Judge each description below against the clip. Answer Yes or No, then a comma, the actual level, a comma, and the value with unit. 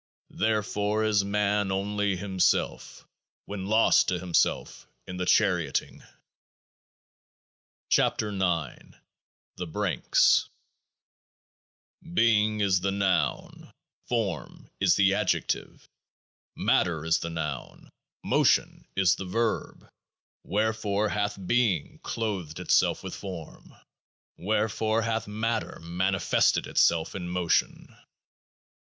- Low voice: Yes, low, 100 Hz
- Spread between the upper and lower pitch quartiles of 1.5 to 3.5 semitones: Yes, average, 2.9 semitones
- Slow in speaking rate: Yes, slow, 100 wpm